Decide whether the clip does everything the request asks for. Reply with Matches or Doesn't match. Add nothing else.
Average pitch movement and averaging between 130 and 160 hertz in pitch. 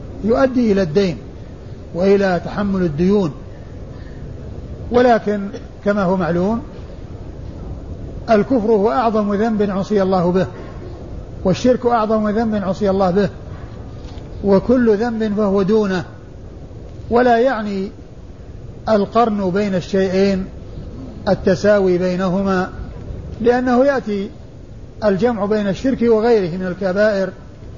Doesn't match